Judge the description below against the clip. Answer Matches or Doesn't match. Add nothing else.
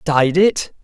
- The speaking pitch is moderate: Matches